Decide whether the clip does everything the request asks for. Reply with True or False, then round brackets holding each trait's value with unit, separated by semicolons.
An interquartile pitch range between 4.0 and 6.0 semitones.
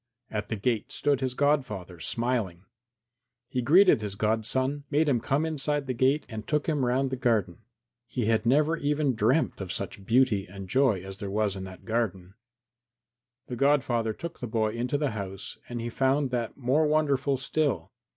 True (4.8 semitones)